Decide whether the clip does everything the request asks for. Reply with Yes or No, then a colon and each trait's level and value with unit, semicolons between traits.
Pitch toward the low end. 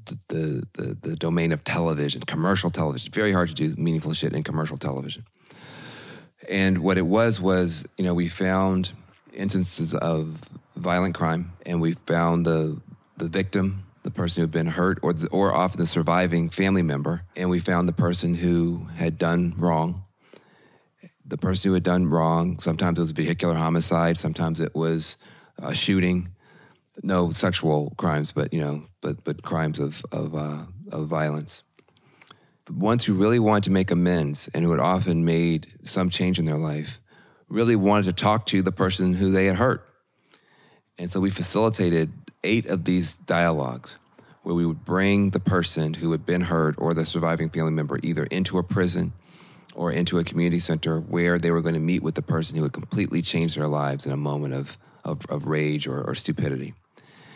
Yes: very low, 85 Hz